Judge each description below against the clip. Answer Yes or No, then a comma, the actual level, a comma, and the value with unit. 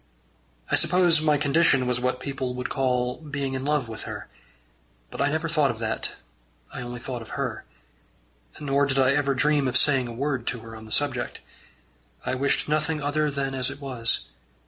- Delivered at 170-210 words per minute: Yes, average, 190 wpm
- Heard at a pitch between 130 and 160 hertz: Yes, low, 135 Hz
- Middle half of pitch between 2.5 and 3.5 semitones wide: Yes, average, 2.8 semitones